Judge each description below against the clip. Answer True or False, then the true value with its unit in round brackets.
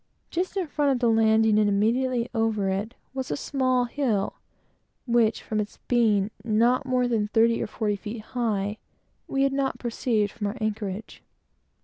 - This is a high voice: True (225 Hz)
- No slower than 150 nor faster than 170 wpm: True (165 wpm)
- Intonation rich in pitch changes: False (3.1 semitones)